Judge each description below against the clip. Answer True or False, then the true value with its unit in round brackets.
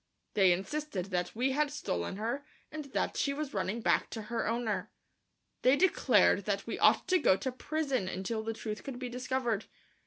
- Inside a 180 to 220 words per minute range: True (185 wpm)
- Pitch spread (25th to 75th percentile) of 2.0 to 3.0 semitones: False (5.0 semitones)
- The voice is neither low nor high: False (240 Hz)